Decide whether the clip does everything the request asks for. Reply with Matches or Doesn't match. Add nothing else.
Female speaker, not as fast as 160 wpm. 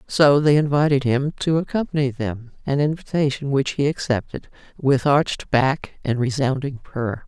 Matches